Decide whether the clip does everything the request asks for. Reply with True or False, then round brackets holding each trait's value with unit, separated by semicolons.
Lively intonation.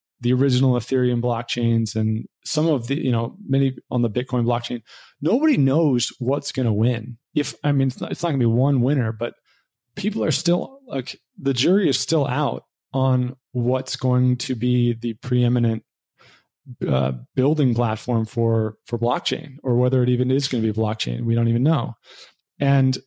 False (2.5 semitones)